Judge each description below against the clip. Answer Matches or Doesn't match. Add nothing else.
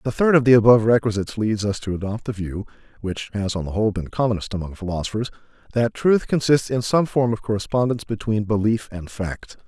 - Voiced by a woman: Doesn't match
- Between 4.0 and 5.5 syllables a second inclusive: Doesn't match